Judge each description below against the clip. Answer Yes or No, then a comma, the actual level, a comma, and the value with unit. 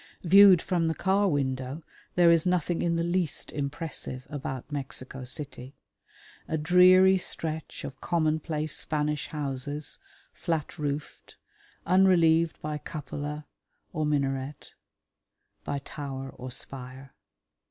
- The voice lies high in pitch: No, medium, 150 Hz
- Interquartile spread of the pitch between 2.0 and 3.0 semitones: No, average, 3.4 semitones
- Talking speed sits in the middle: No, slow, 110 wpm